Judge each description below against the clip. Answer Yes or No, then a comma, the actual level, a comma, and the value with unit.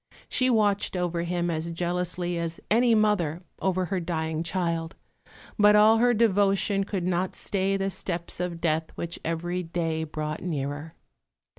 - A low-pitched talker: No, medium, 175 Hz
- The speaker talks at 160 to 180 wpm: No, average, 150 wpm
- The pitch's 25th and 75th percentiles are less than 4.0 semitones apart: Yes, average, 2.9 semitones